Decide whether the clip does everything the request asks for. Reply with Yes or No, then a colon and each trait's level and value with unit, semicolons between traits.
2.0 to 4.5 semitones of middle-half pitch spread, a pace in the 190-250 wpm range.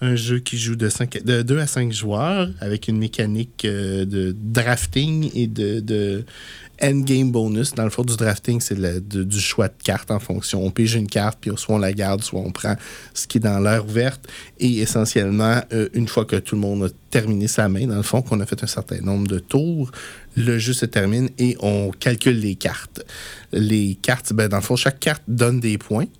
Yes: average, 3.1 semitones; fast, 220 wpm